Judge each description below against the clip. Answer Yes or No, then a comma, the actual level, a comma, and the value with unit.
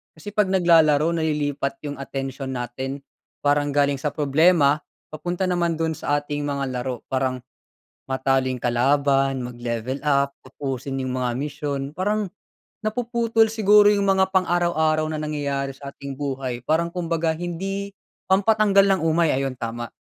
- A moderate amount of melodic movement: Yes, average, 4.6 semitones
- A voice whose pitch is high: No, medium, 145 Hz